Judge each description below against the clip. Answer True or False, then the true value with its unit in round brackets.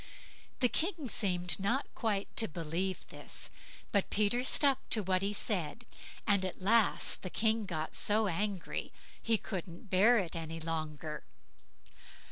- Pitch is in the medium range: False (195 Hz)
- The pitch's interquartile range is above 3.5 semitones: True (4.3 semitones)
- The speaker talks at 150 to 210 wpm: False (140 wpm)